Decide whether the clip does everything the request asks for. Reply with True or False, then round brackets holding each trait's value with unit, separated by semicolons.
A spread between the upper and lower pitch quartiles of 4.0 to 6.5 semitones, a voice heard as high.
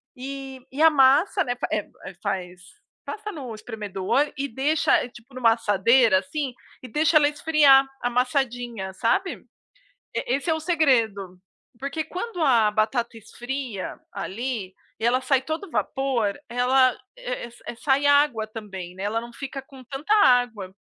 True (4.3 semitones; 255 Hz)